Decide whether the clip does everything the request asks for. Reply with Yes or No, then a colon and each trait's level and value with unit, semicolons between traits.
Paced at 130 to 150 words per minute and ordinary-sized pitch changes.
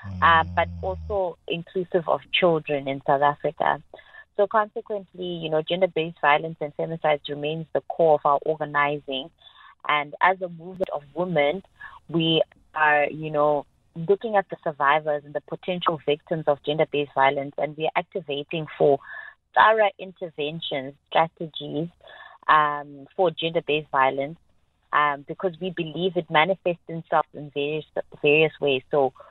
Yes: average, 140 wpm; average, 3.4 semitones